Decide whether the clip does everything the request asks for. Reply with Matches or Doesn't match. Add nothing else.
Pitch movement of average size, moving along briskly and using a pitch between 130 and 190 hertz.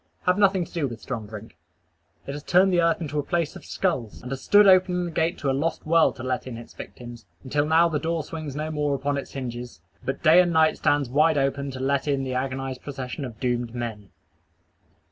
Matches